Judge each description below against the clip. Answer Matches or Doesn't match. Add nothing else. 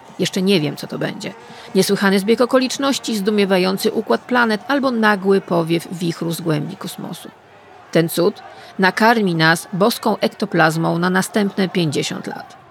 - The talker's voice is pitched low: Doesn't match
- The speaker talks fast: Doesn't match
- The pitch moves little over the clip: Doesn't match